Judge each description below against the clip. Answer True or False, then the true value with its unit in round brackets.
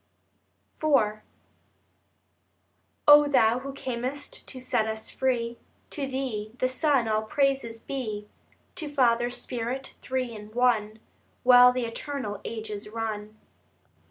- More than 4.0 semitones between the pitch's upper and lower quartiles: False (3.4 semitones)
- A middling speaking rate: False (115 wpm)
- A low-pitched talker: False (245 Hz)